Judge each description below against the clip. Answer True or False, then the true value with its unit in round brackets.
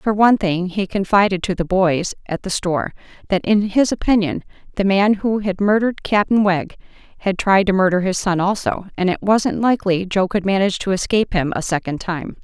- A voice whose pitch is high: True (195 Hz)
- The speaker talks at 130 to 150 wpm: False (205 wpm)